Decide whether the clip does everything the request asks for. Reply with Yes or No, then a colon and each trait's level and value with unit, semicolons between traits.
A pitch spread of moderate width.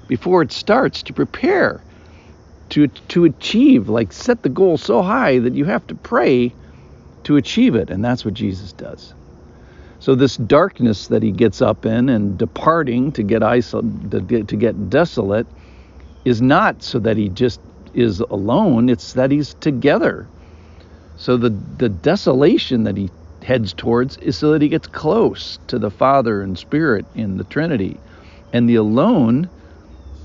No: wide, 5.7 semitones